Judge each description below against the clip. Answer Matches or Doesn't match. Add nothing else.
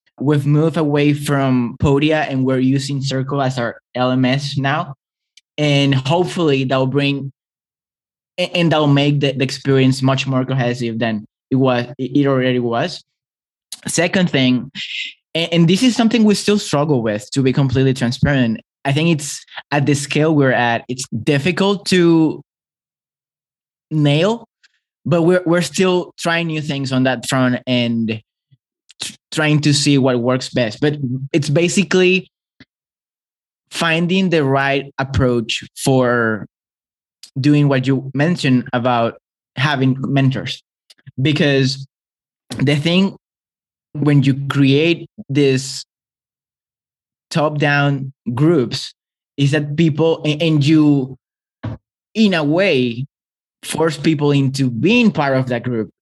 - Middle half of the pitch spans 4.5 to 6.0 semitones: Doesn't match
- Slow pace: Matches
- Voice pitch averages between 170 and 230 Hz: Doesn't match